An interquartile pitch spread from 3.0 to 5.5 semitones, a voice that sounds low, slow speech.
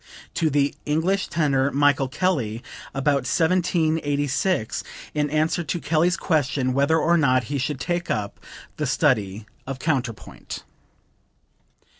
No: average, 3.6 semitones; medium, 145 Hz; slow, 125 wpm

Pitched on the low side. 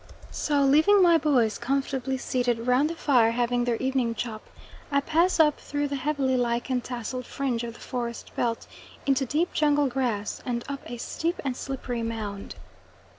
No: very high, 260 Hz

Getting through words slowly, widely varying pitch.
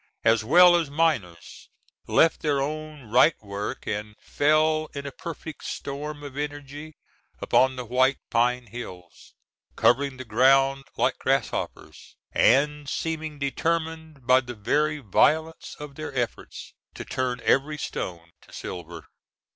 No: slow, 130 wpm; average, 3.9 semitones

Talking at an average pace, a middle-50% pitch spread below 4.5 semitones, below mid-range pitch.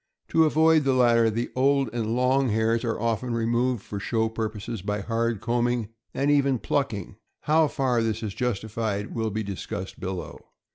Yes: average, 170 wpm; average, 2.7 semitones; low, 115 Hz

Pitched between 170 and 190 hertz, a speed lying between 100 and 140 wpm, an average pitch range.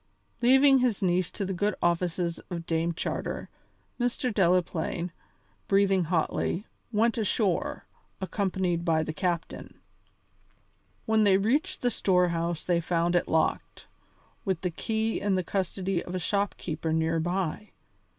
Yes: medium, 185 Hz; slow, 135 wpm; average, 3.2 semitones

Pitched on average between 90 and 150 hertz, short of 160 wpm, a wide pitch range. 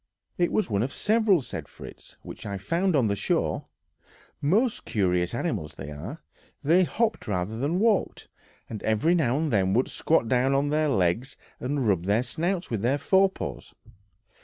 No: low, 135 Hz; average, 175 wpm; wide, 8.7 semitones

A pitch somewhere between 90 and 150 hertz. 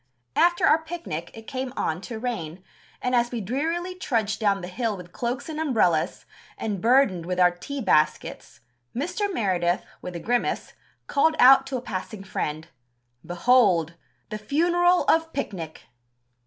No: high, 230 Hz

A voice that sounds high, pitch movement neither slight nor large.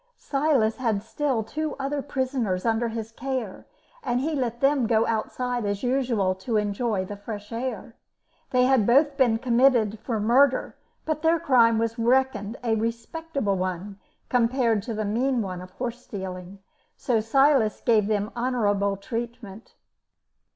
Yes: high, 230 Hz; average, 3.7 semitones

